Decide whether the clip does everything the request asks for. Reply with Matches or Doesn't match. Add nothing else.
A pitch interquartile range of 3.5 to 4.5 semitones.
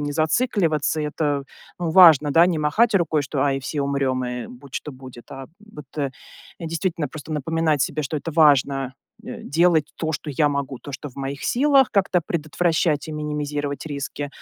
Doesn't match